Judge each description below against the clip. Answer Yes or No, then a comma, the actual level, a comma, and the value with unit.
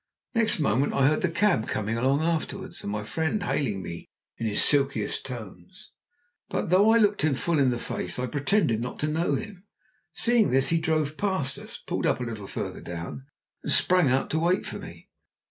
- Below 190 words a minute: No, fast, 205 wpm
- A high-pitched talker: No, medium, 145 Hz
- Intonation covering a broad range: Yes, wide, 6.8 semitones